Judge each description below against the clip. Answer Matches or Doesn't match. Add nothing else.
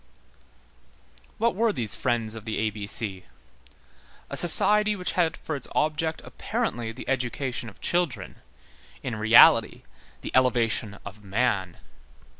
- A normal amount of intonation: Doesn't match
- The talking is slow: Matches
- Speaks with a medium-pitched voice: Doesn't match